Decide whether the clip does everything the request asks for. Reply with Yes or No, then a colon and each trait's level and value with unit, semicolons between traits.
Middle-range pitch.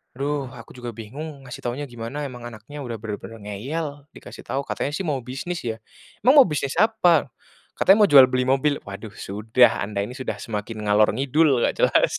No: low, 130 Hz